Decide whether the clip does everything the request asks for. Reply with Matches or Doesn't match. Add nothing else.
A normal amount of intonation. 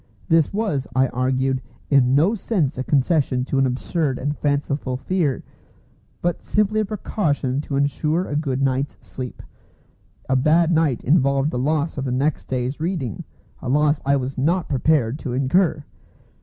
Matches